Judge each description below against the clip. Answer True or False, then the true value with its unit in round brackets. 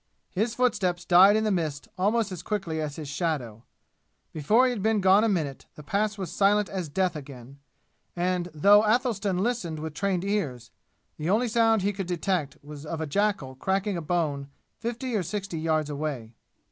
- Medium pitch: True (180 Hz)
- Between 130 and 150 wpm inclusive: False (185 wpm)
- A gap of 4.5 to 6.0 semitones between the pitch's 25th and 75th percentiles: True (5.3 semitones)